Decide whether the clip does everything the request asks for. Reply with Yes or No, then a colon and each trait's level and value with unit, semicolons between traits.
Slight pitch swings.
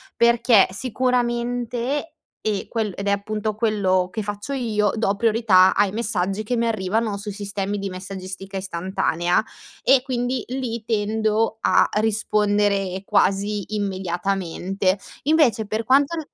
No: average, 3.1 semitones